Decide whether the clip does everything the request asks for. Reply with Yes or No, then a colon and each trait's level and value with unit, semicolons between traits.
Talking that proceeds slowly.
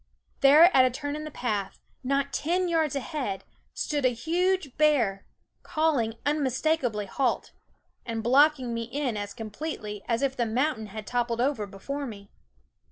No: average, 160 wpm